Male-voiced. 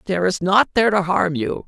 Yes: male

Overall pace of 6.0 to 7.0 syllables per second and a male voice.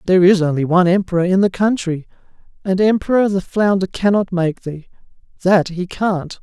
No: 5.5 syllables/s; male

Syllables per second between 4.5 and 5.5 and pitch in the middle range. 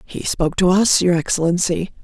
Yes: 5.4 syllables/s; medium, 175 Hz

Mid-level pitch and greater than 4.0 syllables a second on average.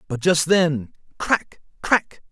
No: medium, 160 Hz; 3.1 syllables/s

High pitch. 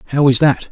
No: low, 135 Hz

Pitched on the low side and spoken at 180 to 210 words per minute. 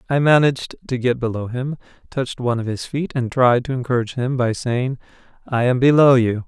Yes: low, 125 Hz; fast, 205 wpm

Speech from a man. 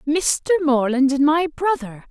No: female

